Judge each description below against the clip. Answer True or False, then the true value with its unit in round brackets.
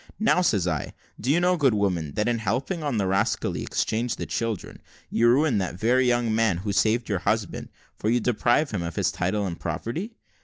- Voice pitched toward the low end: True (110 Hz)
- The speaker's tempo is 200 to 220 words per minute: True (205 wpm)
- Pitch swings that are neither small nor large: True (4.3 semitones)